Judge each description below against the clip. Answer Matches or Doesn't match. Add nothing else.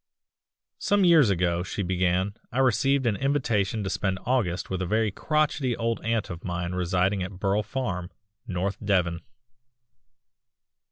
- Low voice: Matches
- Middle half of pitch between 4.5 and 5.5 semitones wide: Matches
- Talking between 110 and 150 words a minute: Matches